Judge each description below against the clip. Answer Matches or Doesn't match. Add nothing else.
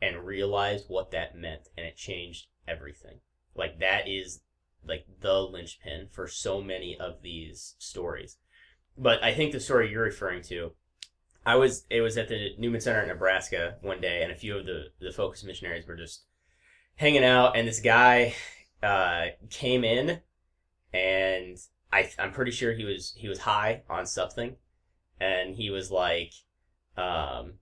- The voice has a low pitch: Matches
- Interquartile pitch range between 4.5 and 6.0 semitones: Matches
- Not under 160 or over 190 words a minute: Matches